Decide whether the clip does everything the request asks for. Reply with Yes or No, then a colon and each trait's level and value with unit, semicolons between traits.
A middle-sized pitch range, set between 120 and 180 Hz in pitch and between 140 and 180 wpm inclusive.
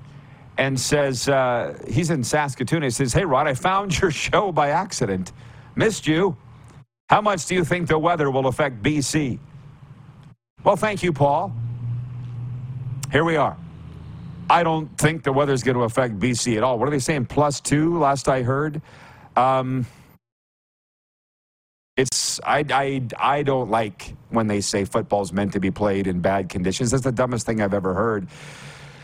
Yes: average, 3.6 semitones; low, 135 Hz; average, 165 wpm